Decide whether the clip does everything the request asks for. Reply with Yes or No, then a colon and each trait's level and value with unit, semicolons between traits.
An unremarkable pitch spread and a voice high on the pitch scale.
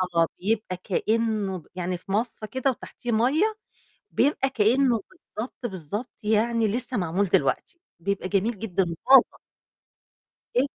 Yes: average, 4.2 semitones; high, 220 Hz